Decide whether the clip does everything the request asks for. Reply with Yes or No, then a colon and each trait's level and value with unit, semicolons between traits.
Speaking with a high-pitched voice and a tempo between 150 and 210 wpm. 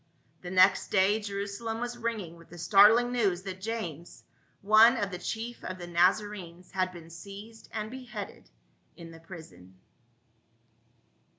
Yes: high, 195 Hz; average, 155 wpm